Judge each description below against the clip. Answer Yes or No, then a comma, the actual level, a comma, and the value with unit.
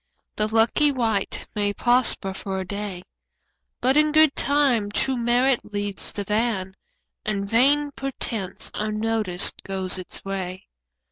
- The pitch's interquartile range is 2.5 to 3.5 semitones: No, average, 4.3 semitones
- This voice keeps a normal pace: No, slow, 130 wpm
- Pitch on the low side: No, high, 215 Hz